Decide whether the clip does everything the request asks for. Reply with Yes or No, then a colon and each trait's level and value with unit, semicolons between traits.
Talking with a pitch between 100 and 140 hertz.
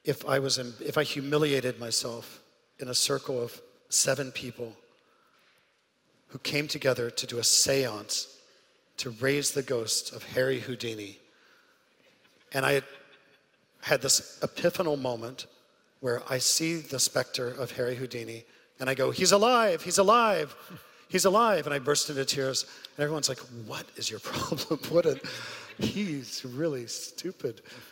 Yes: low, 135 Hz